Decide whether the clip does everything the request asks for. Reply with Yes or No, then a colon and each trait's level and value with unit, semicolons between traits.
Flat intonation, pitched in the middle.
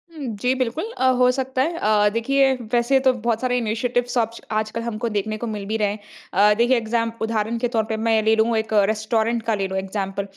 No: narrow, 2.2 semitones; high, 230 Hz